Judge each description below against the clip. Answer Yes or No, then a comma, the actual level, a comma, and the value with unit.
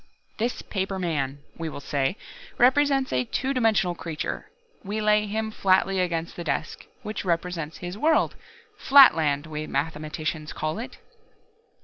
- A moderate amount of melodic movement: No, wide, 5.7 semitones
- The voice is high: No, medium, 180 Hz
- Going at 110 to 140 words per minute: Yes, slow, 135 wpm